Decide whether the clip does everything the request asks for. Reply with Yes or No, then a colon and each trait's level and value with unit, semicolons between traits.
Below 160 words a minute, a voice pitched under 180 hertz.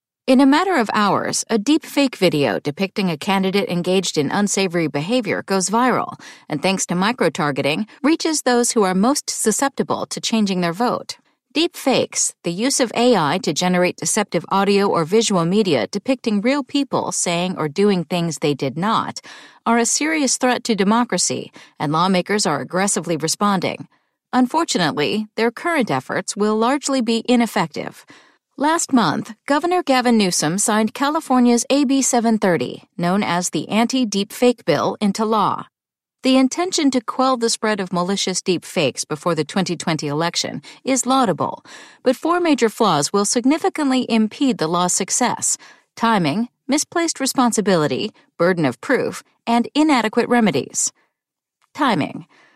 No: average, 145 wpm; high, 220 Hz